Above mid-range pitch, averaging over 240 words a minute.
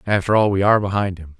No: low, 100 Hz; fast, 260 wpm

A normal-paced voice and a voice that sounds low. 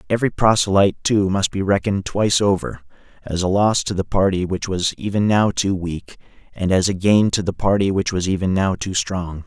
No: fast, 210 wpm; very low, 95 Hz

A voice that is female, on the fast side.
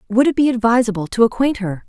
Yes: female; fast, 225 wpm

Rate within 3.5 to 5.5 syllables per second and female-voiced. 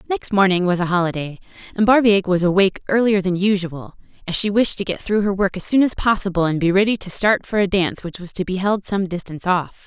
No: 6.1 syllables/s; female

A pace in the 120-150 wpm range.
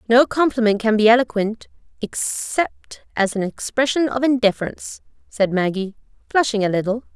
Yes: slow, 135 wpm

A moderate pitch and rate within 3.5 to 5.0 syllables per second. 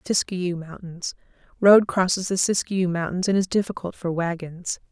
Yes: medium, 180 Hz; 4.8 syllables/s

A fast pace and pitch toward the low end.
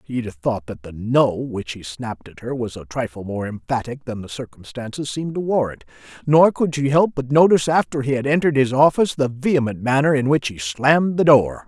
Yes: fast, 215 wpm; low, 130 Hz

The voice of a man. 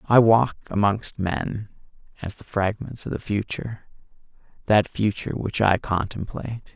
Yes: male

